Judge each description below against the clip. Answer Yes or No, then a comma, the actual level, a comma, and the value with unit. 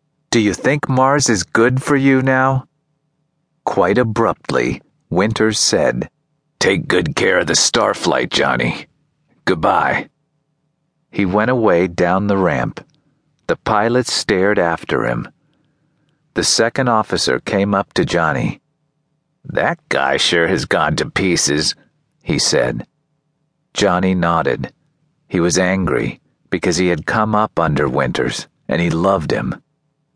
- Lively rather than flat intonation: Yes, wide, 7.7 semitones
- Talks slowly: Yes, slow, 125 wpm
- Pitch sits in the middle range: No, low, 125 Hz